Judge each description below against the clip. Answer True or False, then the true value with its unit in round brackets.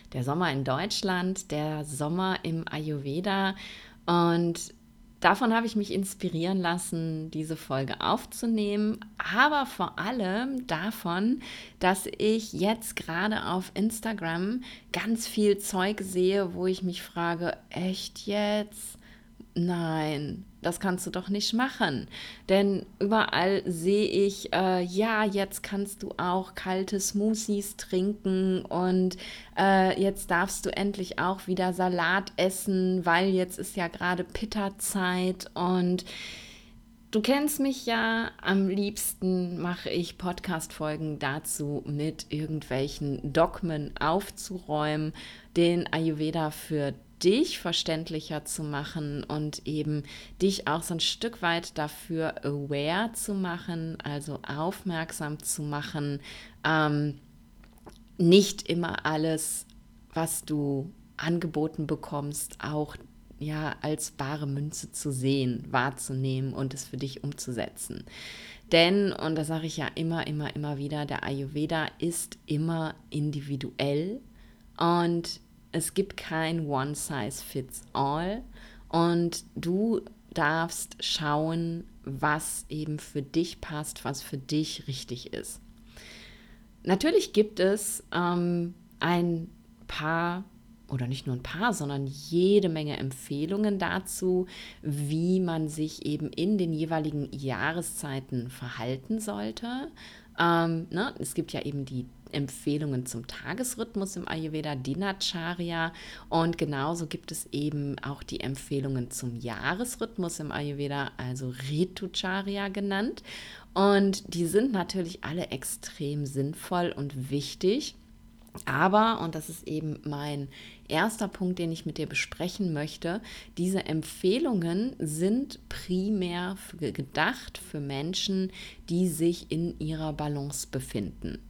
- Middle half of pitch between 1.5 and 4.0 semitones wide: False (4.5 semitones)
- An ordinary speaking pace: False (115 wpm)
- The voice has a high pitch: False (170 Hz)